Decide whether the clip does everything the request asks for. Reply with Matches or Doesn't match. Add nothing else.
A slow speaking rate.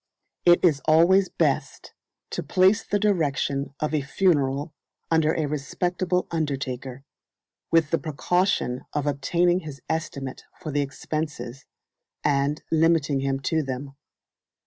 Matches